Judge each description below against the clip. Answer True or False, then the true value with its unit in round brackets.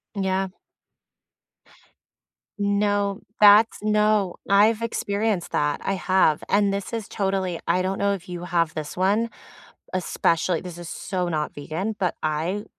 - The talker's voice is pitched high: True (195 Hz)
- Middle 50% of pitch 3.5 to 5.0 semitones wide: False (2.7 semitones)